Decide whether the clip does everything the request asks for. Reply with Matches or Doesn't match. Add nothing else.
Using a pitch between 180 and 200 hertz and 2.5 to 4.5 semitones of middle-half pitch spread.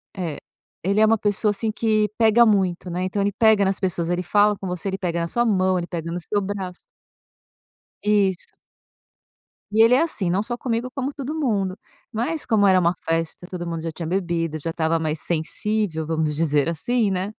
Matches